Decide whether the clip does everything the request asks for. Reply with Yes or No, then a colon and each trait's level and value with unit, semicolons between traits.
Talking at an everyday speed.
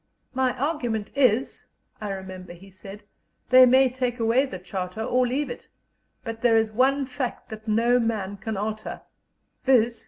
Yes: average, 160 wpm